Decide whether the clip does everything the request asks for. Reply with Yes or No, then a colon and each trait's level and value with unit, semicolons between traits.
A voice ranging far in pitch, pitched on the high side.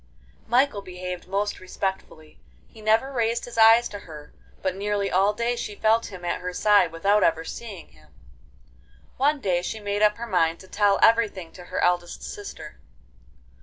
No: average, 3.8 semitones; high, 200 Hz